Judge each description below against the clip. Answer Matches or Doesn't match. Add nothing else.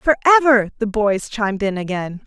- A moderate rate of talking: Matches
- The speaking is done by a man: Doesn't match